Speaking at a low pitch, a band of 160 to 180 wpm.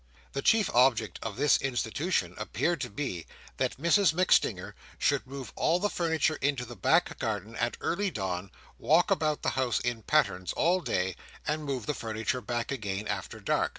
Yes: low, 130 Hz; average, 175 wpm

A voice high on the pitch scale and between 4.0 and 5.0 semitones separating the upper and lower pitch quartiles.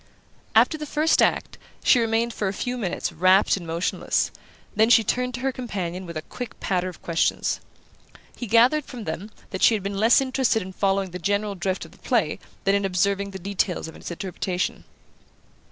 Yes: high, 200 Hz; average, 4.3 semitones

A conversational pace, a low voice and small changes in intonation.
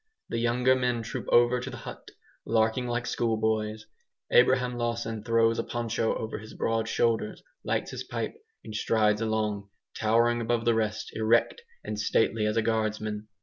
Yes: average, 160 wpm; low, 115 Hz; narrow, 1.5 semitones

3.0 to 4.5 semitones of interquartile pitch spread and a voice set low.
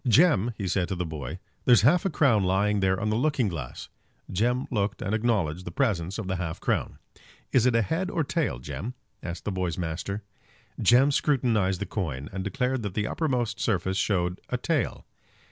No: average, 5.3 semitones; low, 105 Hz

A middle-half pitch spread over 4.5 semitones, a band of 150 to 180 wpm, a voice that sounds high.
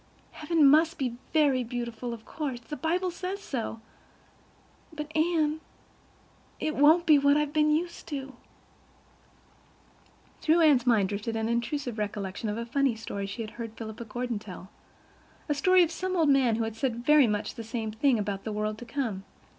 Yes: wide, 5.4 semitones; average, 170 wpm; very high, 250 Hz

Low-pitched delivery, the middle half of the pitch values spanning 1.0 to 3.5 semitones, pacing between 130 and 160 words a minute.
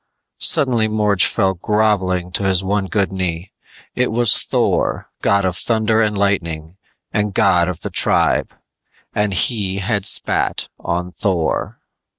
Yes: low, 100 Hz; narrow, 2.6 semitones; average, 140 wpm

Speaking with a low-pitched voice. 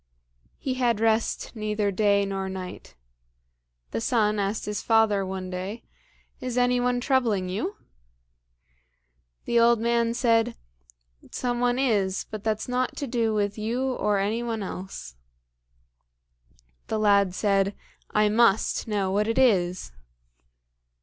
No: high, 215 Hz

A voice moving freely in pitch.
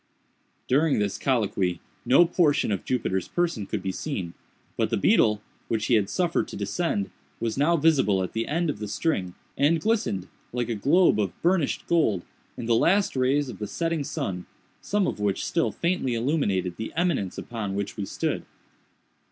Yes: wide, 8.4 semitones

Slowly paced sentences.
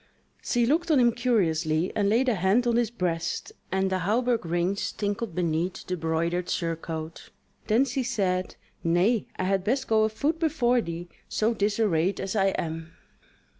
No: average, 165 wpm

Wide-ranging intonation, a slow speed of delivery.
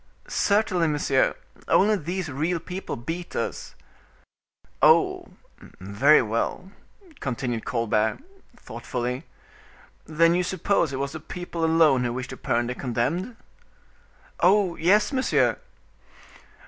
Yes: wide, 6.4 semitones; slow, 110 wpm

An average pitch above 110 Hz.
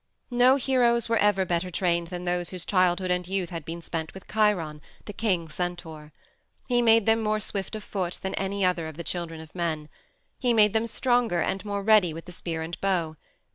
Yes: medium, 185 Hz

